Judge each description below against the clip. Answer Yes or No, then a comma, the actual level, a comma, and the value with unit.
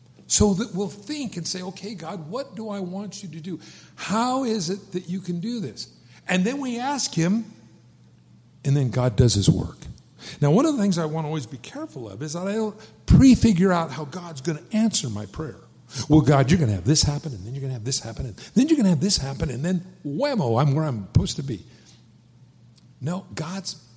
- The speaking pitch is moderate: Yes, medium, 165 Hz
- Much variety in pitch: Yes, wide, 7.2 semitones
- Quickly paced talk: Yes, fast, 235 wpm